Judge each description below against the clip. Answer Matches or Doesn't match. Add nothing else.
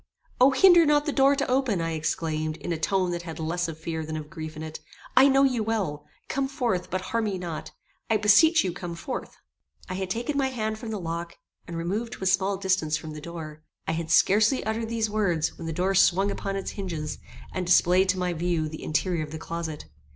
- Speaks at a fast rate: Matches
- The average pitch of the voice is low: Doesn't match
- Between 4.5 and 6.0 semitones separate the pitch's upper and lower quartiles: Matches